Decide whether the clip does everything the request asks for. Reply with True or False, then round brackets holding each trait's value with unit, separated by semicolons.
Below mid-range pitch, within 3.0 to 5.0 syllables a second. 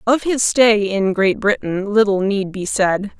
False (205 Hz; 4.0 syllables/s)